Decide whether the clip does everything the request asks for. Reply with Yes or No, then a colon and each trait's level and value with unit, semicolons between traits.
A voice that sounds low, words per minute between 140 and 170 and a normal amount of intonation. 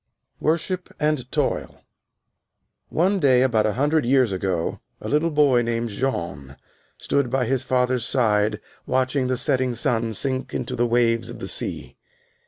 Yes: low, 125 Hz; average, 155 wpm; average, 3.0 semitones